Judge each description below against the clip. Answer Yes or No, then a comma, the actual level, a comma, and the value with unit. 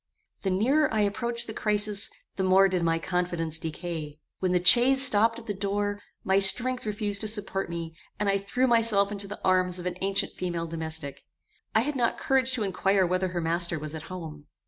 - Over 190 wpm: Yes, average, 200 wpm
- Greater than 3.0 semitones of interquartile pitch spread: Yes, average, 3.6 semitones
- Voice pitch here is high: Yes, high, 195 Hz